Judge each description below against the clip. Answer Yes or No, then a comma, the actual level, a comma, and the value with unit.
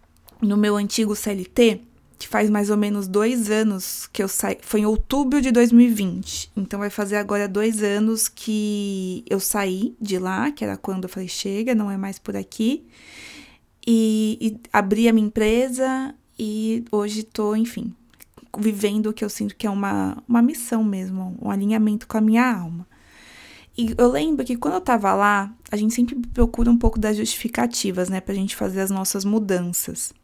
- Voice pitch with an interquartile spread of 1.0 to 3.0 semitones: Yes, narrow, 2.5 semitones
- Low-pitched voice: No, high, 215 Hz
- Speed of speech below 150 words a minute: No, average, 180 wpm